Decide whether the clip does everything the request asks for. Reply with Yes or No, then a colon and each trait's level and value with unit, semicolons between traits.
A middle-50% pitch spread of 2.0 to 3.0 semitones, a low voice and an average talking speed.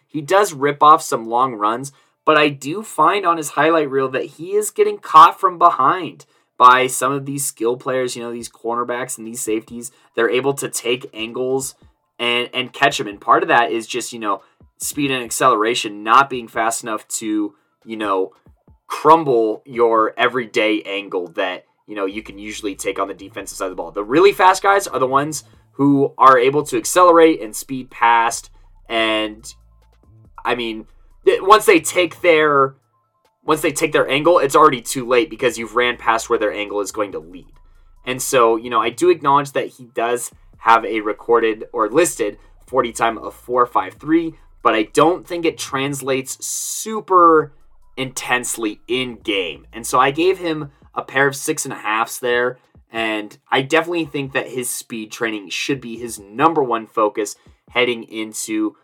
No: average, 5.2 semitones; low, 125 Hz; average, 185 wpm